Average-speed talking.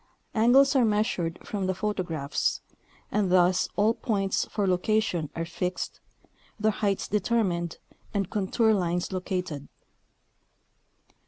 No: slow, 110 wpm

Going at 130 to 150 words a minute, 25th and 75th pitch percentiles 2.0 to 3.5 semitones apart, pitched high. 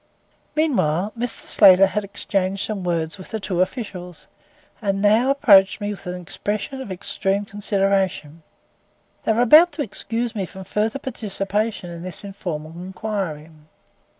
Yes: average, 145 wpm; average, 3.1 semitones; high, 195 Hz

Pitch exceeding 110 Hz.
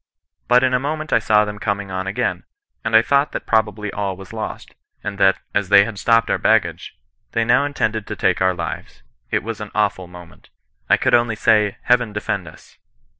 No: low, 105 Hz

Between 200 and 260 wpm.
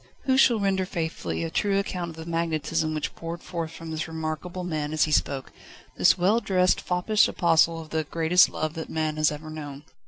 Yes: fast, 205 wpm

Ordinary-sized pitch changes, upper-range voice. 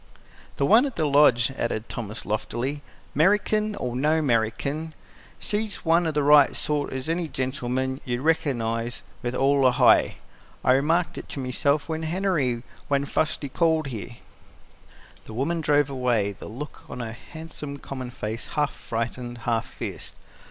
No: average, 4.6 semitones; medium, 140 Hz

